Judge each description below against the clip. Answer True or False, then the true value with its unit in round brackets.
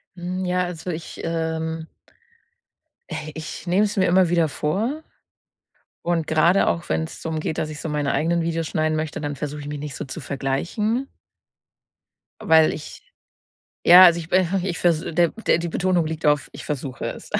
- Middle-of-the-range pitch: True (165 Hz)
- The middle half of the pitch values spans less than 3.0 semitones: True (2.4 semitones)